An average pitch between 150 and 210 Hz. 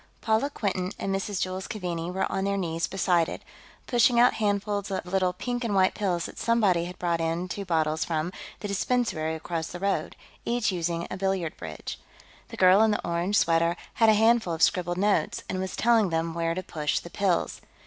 Yes: medium, 185 Hz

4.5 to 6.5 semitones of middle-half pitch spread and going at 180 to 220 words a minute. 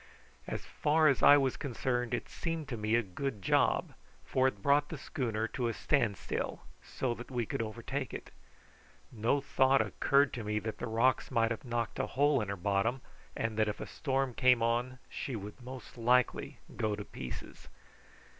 No: average, 3.3 semitones; average, 190 wpm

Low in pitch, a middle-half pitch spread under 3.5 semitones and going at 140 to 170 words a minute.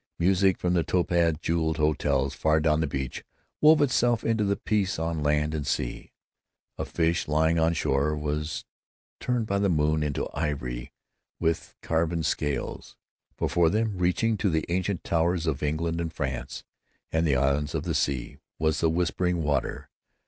Yes: very low, 80 Hz; average, 2.9 semitones; average, 165 wpm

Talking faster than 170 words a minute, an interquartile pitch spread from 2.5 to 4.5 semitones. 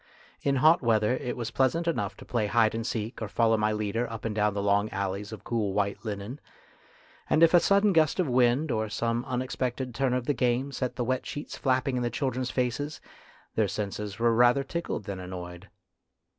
Yes: fast, 205 wpm; average, 3.6 semitones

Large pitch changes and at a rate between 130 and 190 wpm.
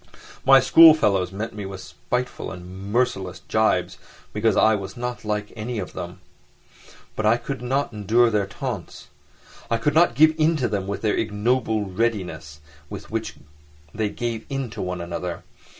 No: average, 4.1 semitones; average, 165 wpm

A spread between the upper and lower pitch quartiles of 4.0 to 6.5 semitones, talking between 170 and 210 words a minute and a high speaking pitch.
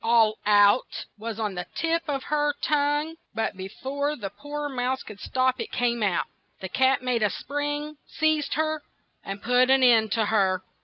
Yes: average, 5.3 semitones; average, 185 wpm; very high, 255 Hz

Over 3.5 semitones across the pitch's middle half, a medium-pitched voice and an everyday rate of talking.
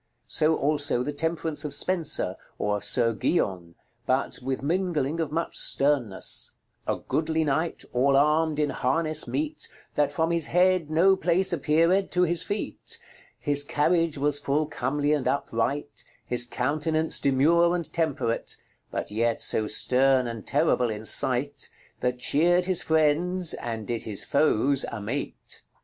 Yes: average, 4.2 semitones; medium, 145 Hz; average, 145 wpm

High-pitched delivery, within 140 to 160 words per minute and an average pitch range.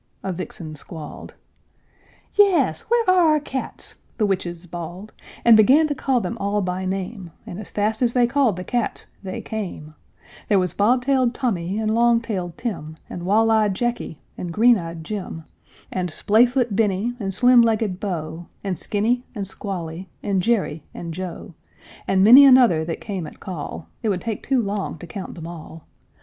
No: high, 205 Hz; average, 175 wpm; average, 5.0 semitones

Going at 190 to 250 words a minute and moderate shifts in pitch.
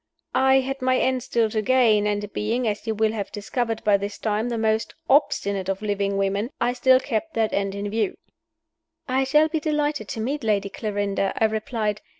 Yes: average, 195 wpm; average, 3.9 semitones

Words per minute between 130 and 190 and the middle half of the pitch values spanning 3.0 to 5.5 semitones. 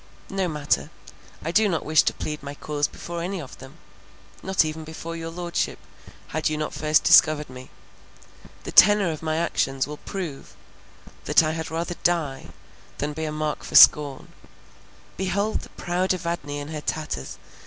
No: average, 165 wpm; narrow, 2.5 semitones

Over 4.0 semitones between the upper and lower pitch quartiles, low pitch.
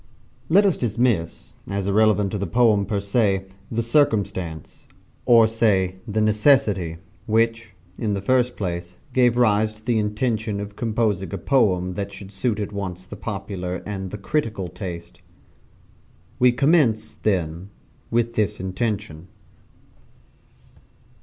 No: average, 3.2 semitones; low, 105 Hz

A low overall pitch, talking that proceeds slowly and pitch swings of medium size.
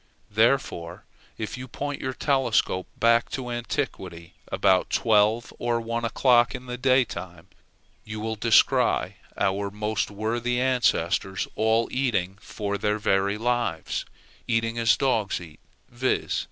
Yes: low, 115 Hz; slow, 125 wpm; average, 3.3 semitones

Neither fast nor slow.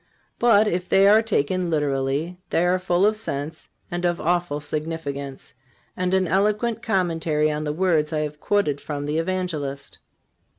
Yes: average, 160 wpm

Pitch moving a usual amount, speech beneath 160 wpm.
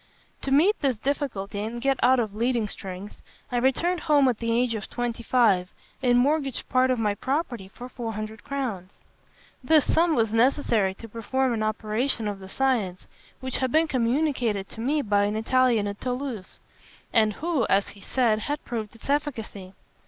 No: average, 4.0 semitones; average, 180 wpm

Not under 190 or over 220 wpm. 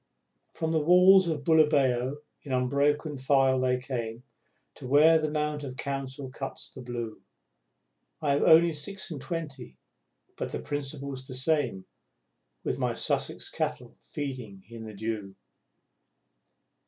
No: slow, 135 wpm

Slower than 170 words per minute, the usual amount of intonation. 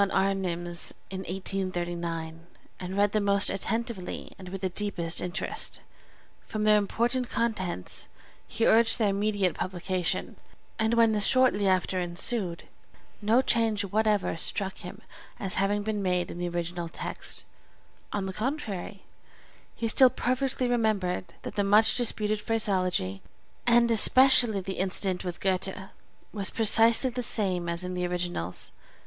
Yes: average, 140 wpm; average, 3.5 semitones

